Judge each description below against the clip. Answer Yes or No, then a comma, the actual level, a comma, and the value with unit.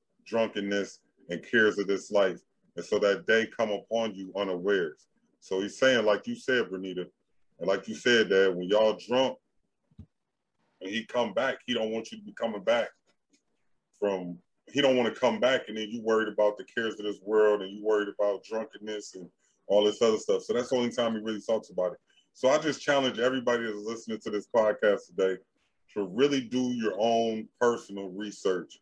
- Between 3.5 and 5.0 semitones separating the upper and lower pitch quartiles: No, average, 2.9 semitones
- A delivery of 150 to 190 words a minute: No, average, 200 wpm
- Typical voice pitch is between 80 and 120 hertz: Yes, low, 110 Hz